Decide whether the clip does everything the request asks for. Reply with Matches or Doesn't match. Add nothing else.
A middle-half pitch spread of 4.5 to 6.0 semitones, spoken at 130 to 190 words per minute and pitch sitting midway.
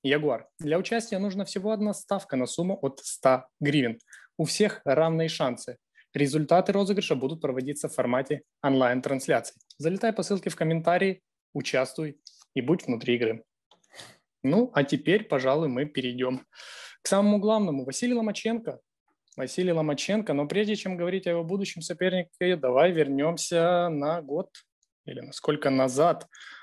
Matches